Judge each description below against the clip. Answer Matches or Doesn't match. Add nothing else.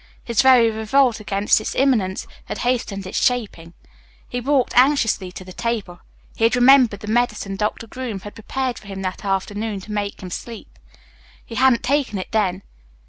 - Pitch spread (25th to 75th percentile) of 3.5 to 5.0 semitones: Matches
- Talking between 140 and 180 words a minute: Matches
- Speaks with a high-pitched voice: Matches